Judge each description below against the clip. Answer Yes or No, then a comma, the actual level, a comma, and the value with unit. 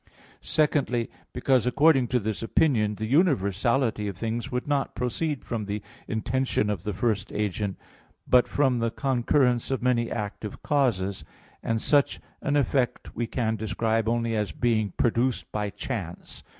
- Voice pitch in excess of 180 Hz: No, low, 115 Hz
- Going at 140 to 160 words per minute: Yes, average, 150 wpm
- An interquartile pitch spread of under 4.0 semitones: Yes, average, 3.5 semitones